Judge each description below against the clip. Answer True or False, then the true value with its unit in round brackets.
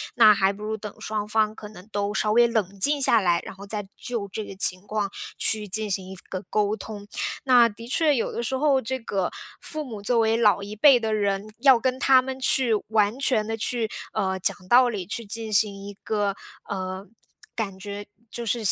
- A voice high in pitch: True (215 Hz)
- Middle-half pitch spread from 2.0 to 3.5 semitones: True (2.8 semitones)